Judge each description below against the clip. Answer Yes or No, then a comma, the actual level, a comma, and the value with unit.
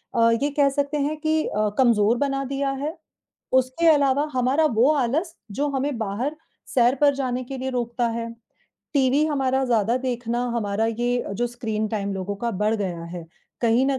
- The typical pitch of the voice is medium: No, very high, 250 Hz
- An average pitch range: Yes, average, 3.6 semitones